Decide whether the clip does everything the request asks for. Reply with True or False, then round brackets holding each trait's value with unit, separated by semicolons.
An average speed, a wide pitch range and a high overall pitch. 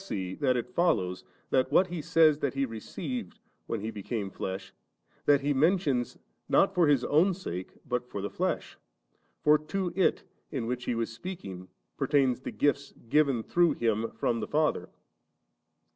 False (175 wpm; 5.8 semitones; 135 Hz)